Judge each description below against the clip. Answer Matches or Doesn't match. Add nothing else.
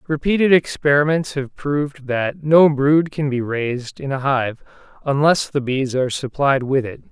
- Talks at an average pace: Matches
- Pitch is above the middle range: Doesn't match